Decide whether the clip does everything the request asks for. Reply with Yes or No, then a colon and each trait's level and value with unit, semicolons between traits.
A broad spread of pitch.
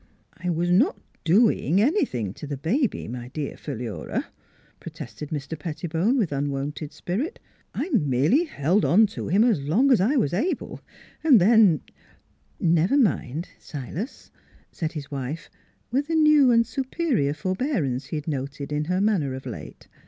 Yes: wide, 8.3 semitones